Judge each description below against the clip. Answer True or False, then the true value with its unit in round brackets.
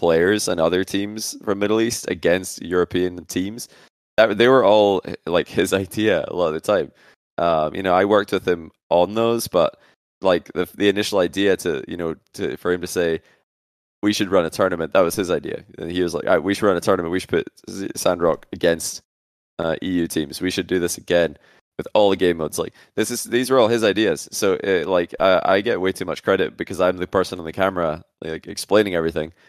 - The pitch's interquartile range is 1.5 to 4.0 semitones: True (3.3 semitones)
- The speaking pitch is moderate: False (90 Hz)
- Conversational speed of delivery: False (225 wpm)